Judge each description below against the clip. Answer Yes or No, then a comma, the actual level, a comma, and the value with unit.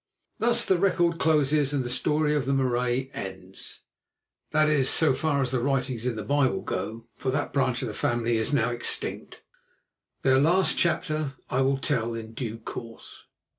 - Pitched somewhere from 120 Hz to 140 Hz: Yes, low, 135 Hz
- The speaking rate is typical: Yes, average, 170 wpm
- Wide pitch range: No, average, 4.0 semitones